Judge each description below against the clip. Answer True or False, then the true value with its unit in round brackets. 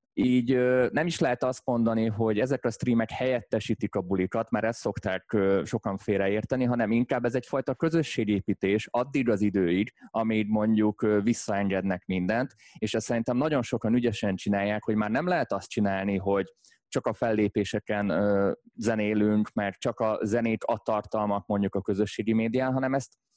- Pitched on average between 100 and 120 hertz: True (110 Hz)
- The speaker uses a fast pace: True (165 wpm)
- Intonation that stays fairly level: False (3.0 semitones)